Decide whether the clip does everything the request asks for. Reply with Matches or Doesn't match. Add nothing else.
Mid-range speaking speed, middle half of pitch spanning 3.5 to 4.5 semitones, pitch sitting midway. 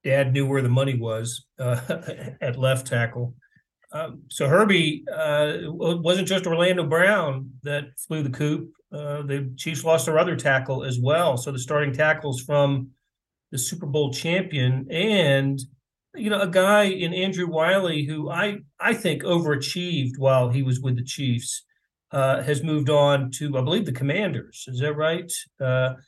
Matches